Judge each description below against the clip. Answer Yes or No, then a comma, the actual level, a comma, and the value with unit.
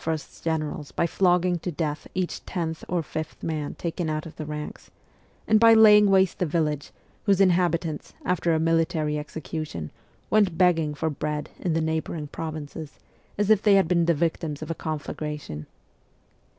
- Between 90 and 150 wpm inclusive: No, average, 165 wpm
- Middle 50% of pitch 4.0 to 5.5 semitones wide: No, average, 2.7 semitones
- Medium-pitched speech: Yes, medium, 160 Hz